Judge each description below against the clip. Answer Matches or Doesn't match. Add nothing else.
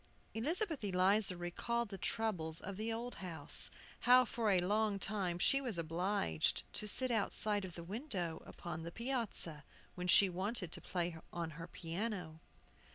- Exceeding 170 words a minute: Doesn't match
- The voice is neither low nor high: Doesn't match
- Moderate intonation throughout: Matches